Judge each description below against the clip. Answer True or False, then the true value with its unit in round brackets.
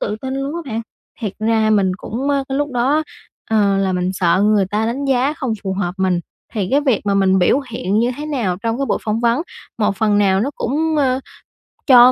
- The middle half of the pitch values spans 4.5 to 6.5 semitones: True (5.2 semitones)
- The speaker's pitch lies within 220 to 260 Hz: True (225 Hz)